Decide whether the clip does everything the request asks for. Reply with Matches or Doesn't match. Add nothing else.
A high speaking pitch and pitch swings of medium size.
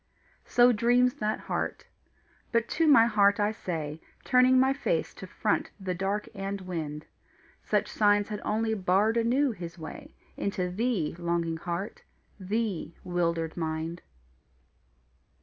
Matches